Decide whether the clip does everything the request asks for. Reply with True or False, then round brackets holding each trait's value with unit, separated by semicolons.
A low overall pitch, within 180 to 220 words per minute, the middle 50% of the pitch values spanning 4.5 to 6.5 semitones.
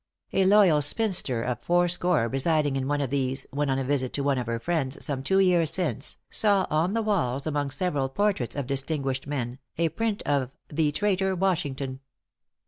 False (145 Hz; 190 wpm; 5.1 semitones)